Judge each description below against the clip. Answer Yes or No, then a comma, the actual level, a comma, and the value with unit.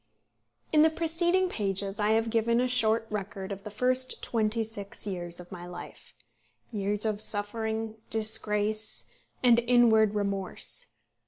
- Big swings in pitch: No, narrow, 2.6 semitones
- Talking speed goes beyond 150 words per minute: No, average, 140 wpm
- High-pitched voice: Yes, high, 220 Hz